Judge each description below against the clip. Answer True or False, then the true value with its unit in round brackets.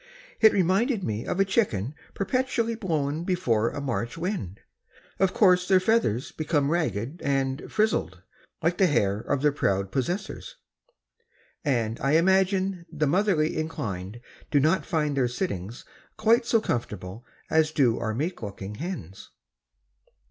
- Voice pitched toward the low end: False (155 Hz)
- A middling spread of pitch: False (8.4 semitones)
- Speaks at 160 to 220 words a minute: False (140 wpm)